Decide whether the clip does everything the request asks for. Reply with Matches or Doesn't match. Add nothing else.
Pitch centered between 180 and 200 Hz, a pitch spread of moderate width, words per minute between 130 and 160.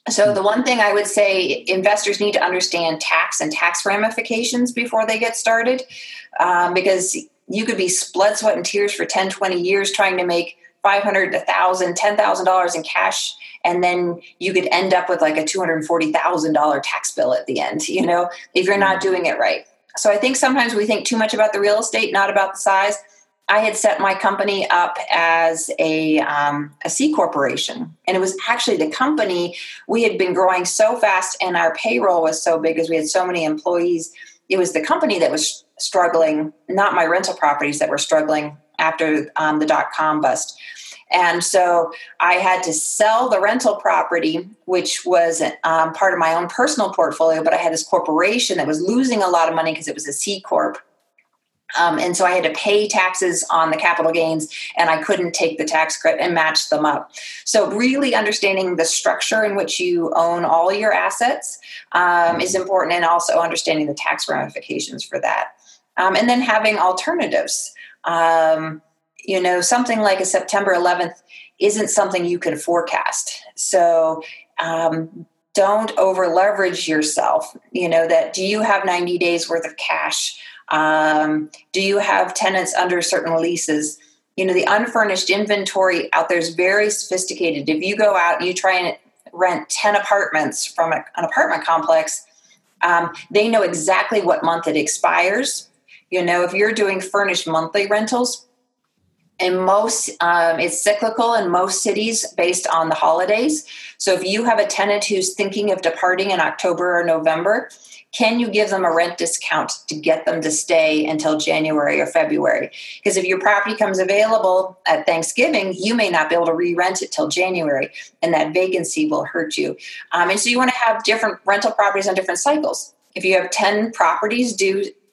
Doesn't match